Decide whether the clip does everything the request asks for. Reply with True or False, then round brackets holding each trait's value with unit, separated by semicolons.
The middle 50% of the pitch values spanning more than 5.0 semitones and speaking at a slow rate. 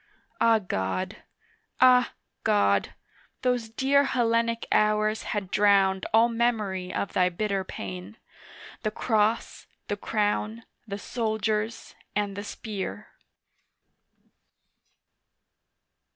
False (2.7 semitones; 95 wpm)